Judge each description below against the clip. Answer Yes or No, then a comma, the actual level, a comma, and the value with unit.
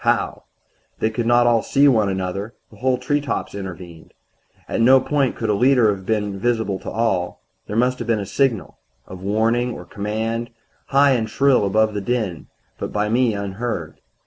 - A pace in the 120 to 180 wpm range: Yes, average, 175 wpm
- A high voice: No, low, 110 Hz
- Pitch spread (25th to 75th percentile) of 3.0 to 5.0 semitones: Yes, average, 3.5 semitones